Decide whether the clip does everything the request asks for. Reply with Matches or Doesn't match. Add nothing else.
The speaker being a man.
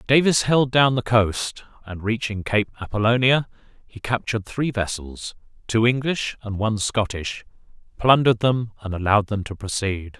Matches